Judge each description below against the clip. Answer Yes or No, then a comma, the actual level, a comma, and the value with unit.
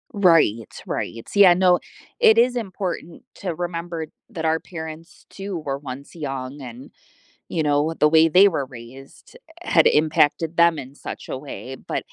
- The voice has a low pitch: No, medium, 160 Hz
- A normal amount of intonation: Yes, average, 4.1 semitones